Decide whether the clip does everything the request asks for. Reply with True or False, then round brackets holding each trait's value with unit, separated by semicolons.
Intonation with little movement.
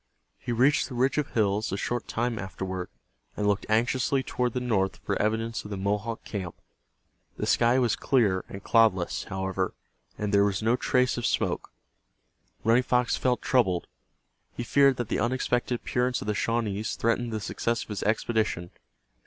False (3.4 semitones)